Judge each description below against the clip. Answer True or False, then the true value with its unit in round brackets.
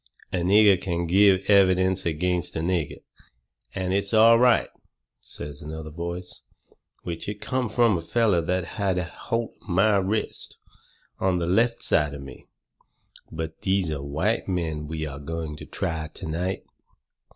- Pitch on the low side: True (90 Hz)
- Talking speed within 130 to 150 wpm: False (160 wpm)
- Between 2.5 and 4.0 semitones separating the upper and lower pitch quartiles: True (3.7 semitones)